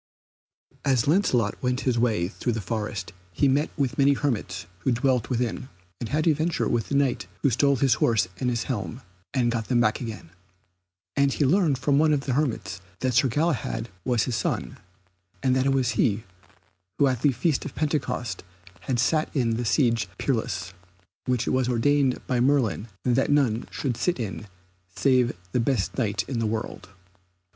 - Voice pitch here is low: Yes, low, 125 Hz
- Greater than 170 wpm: Yes, average, 180 wpm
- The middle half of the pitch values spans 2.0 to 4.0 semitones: Yes, average, 3.4 semitones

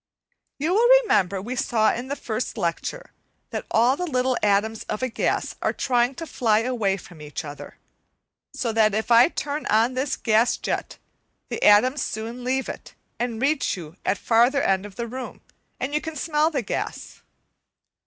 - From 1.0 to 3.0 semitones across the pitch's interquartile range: No, average, 4.2 semitones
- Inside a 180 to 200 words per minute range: Yes, average, 185 wpm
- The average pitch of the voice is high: Yes, high, 240 Hz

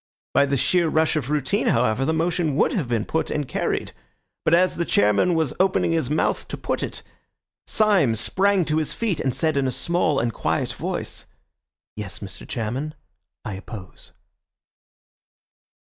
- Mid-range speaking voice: Yes, medium, 150 Hz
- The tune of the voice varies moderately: No, wide, 5.7 semitones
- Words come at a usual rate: Yes, average, 165 wpm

